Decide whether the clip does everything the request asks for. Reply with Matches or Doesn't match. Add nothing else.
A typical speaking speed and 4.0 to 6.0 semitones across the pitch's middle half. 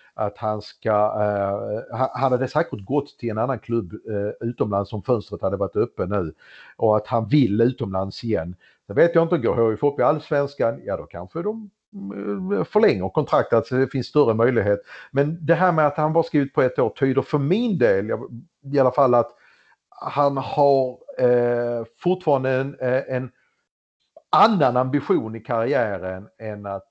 Matches